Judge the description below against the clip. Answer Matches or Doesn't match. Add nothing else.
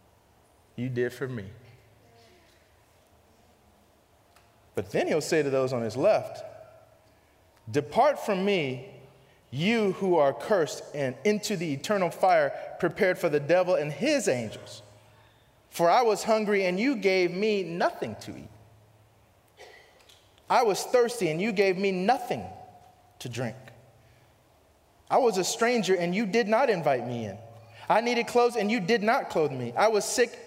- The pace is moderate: Matches